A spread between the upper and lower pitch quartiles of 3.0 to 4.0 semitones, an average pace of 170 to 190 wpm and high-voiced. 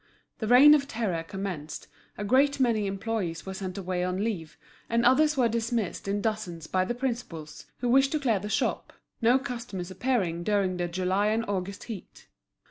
No: average, 4.7 semitones; average, 180 wpm; high, 210 Hz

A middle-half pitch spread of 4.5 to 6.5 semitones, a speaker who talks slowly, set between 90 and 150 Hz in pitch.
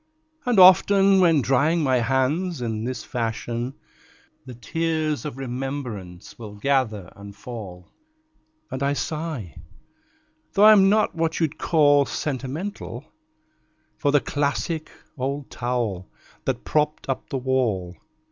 Yes: average, 5.0 semitones; slow, 120 wpm; low, 135 Hz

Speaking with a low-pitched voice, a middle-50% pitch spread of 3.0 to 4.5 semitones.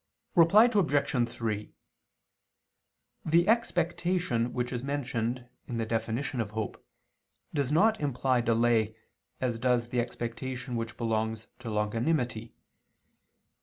Yes: low, 120 Hz; average, 3.9 semitones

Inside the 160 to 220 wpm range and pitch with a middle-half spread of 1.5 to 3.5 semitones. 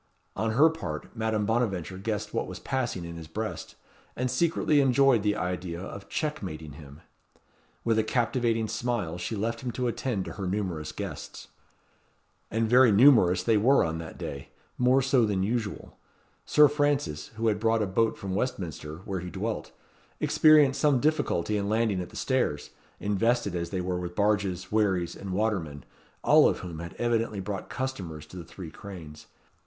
No: average, 170 wpm; average, 5.1 semitones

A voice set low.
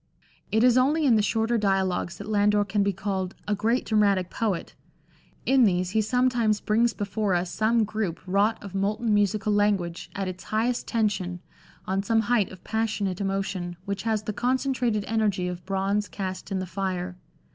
No: high, 205 Hz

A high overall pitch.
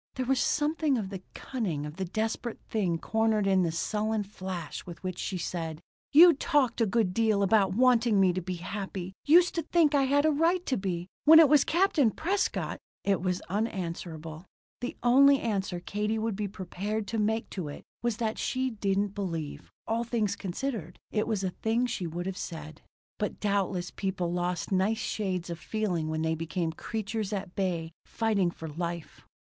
Yes: high, 200 Hz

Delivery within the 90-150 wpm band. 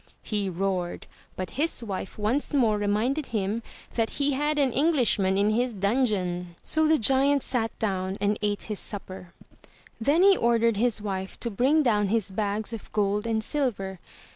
No: average, 170 wpm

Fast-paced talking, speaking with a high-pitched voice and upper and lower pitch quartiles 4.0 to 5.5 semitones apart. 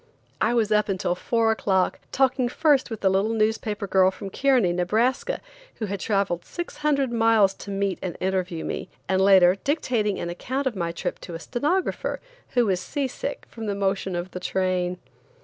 No: average, 185 wpm; high, 205 Hz; average, 4.4 semitones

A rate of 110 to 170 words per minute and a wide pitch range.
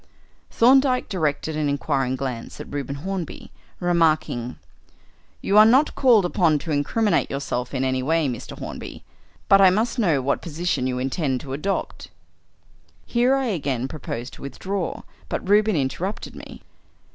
Yes: average, 145 wpm; wide, 6.7 semitones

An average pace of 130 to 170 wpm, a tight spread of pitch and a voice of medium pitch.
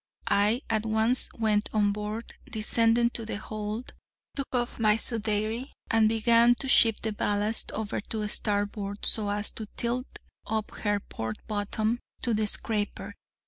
No: average, 150 wpm; narrow, 1.8 semitones; high, 220 Hz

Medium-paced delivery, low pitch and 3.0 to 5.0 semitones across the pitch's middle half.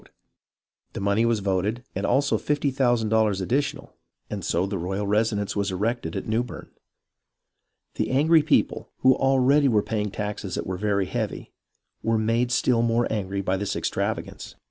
Yes: average, 160 wpm; low, 110 Hz; average, 3.7 semitones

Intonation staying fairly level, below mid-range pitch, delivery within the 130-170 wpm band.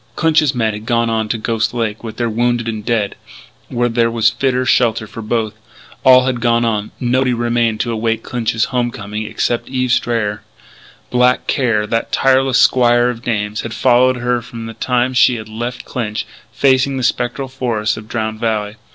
No: narrow, 2.1 semitones; low, 120 Hz; average, 185 wpm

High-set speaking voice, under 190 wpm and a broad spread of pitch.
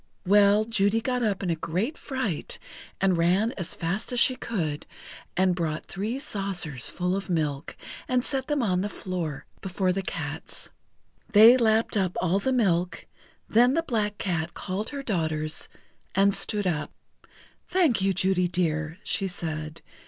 No: high, 195 Hz; average, 160 wpm; average, 4.4 semitones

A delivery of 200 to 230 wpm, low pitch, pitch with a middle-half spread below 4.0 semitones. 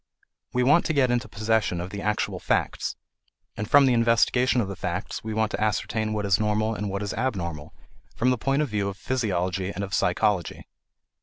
Yes: fast, 205 wpm; low, 110 Hz; average, 3.6 semitones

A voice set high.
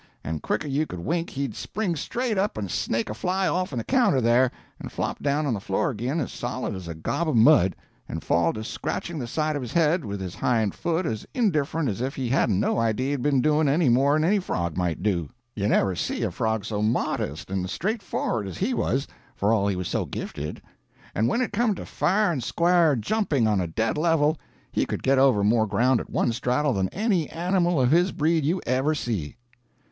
No: low, 130 Hz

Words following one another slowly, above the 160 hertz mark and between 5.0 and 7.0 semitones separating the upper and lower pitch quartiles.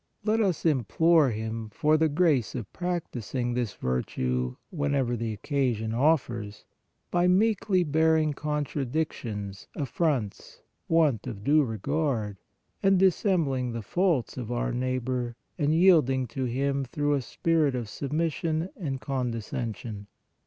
No: slow, 130 wpm; low, 135 Hz; wide, 5.4 semitones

